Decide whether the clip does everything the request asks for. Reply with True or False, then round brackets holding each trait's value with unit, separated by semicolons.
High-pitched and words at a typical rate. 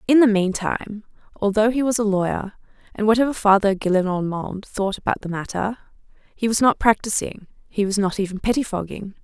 True (205 Hz; 160 wpm)